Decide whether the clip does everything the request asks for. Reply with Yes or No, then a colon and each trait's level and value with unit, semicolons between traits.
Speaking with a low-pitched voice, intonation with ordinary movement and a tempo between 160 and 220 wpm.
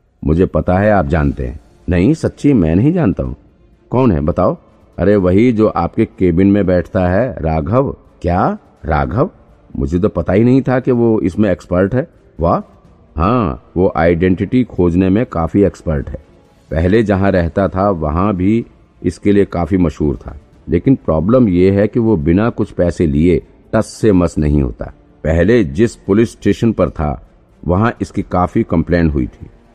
Yes: very low, 95 Hz; average, 4.3 semitones; average, 170 wpm